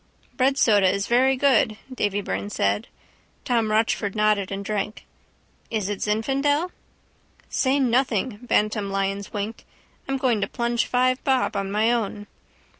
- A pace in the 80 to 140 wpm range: Yes, slow, 135 wpm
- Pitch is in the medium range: No, high, 220 Hz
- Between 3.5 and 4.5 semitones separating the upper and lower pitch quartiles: Yes, average, 4.0 semitones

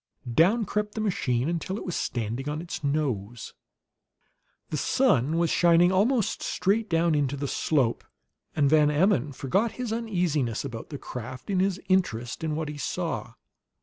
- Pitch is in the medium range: Yes, medium, 155 Hz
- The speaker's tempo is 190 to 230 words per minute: No, average, 160 wpm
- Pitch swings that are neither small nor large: No, wide, 5.9 semitones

